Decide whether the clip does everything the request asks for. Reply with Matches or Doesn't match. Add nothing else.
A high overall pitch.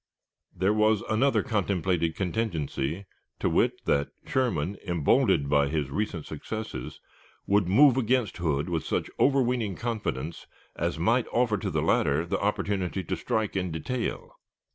Doesn't match